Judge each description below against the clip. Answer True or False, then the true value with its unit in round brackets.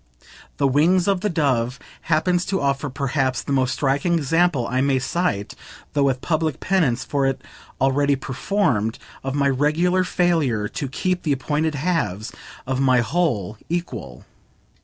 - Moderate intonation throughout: True (4.6 semitones)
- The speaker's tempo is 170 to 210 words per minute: False (150 wpm)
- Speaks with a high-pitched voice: False (140 Hz)